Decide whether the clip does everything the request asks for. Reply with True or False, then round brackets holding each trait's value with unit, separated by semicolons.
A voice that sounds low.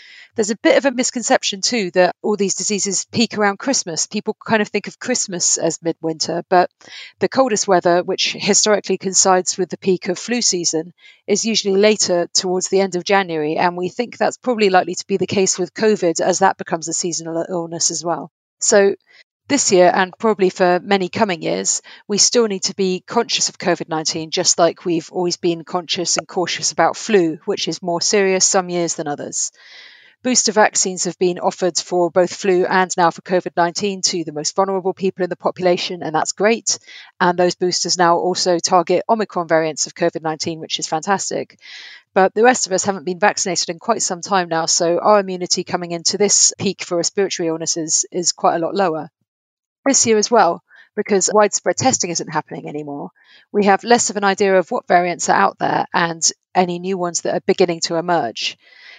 False (185 Hz)